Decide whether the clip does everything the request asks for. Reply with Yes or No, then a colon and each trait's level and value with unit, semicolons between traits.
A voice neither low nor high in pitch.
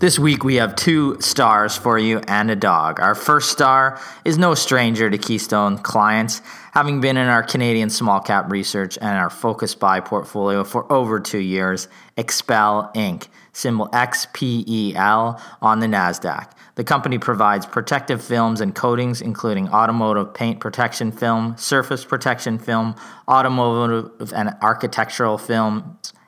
No: low, 115 Hz